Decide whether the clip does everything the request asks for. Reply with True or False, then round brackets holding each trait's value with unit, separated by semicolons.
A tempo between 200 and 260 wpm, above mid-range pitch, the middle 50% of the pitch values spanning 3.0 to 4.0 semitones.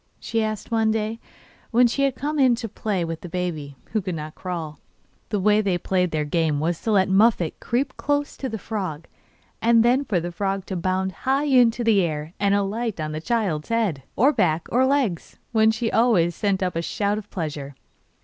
False (205 wpm; 200 Hz; 5.2 semitones)